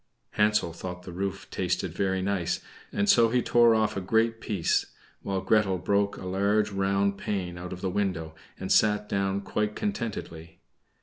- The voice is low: Yes, low, 100 Hz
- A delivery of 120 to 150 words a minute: No, average, 170 wpm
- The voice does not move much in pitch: Yes, narrow, 2.3 semitones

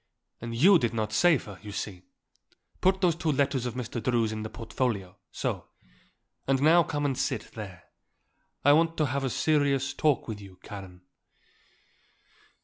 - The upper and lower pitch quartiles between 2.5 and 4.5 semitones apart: No, wide, 5.4 semitones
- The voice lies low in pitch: Yes, low, 125 Hz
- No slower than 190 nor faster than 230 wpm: No, average, 165 wpm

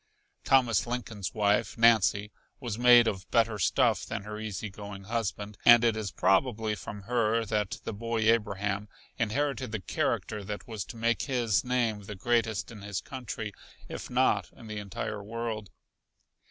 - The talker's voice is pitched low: Yes, low, 110 Hz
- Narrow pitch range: Yes, narrow, 2.3 semitones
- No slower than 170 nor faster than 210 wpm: No, average, 160 wpm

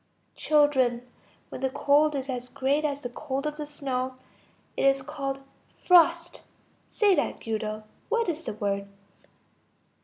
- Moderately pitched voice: No, very high, 275 Hz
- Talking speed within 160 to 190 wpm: No, average, 145 wpm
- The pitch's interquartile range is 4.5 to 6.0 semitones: No, average, 3.1 semitones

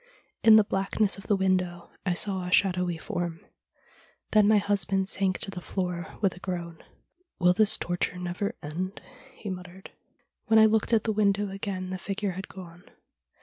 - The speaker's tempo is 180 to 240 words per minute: Yes, average, 190 wpm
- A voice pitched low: No, high, 190 Hz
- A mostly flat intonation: Yes, narrow, 2.3 semitones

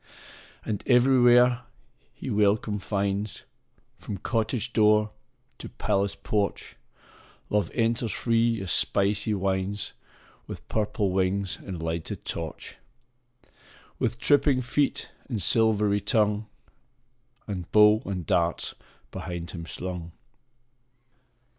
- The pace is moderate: No, slow, 100 wpm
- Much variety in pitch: No, average, 3.0 semitones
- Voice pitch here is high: No, low, 105 Hz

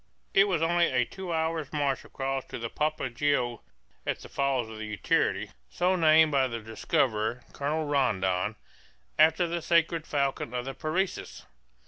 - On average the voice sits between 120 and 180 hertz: Yes, medium, 140 Hz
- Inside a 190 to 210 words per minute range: No, average, 150 wpm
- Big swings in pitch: No, average, 4.9 semitones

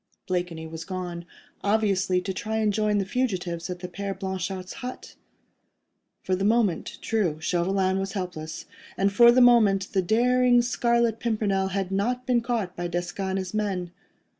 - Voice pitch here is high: Yes, high, 195 Hz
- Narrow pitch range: No, average, 3.4 semitones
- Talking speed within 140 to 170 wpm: Yes, average, 160 wpm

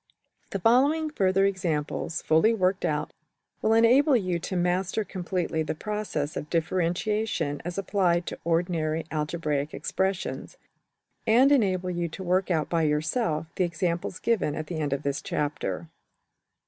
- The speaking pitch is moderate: Yes, medium, 175 Hz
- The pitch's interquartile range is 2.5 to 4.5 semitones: Yes, average, 3.9 semitones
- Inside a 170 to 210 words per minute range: No, average, 145 wpm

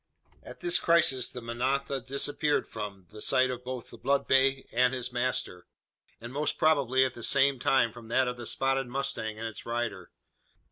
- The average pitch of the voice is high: No, low, 130 Hz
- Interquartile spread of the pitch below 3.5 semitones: Yes, narrow, 2.5 semitones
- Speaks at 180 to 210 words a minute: Yes, average, 185 wpm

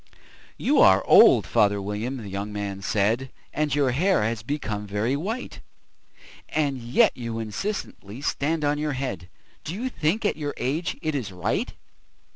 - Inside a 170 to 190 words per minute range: No, average, 160 wpm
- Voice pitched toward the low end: Yes, low, 130 Hz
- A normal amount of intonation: No, wide, 6.5 semitones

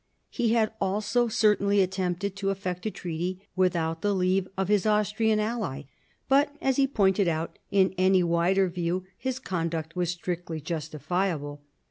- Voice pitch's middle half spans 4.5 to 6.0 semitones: No, average, 3.5 semitones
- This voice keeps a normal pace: Yes, average, 150 wpm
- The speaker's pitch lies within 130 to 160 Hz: No, high, 190 Hz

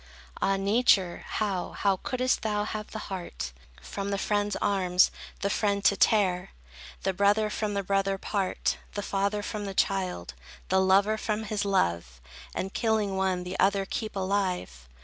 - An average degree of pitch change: No, narrow, 1.6 semitones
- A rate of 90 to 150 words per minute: No, average, 160 wpm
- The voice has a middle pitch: No, high, 200 Hz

